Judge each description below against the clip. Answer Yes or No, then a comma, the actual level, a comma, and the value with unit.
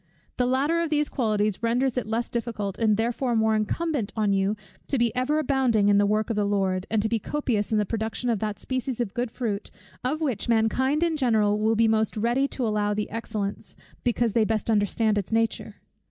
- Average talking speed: No, fast, 210 wpm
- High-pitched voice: Yes, high, 225 Hz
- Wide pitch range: No, average, 3.0 semitones